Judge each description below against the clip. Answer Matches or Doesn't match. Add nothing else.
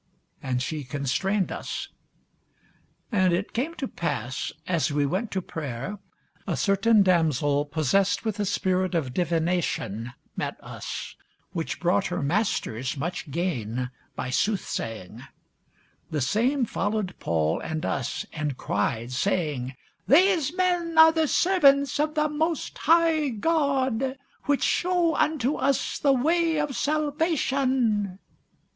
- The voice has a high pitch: Matches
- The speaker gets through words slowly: Matches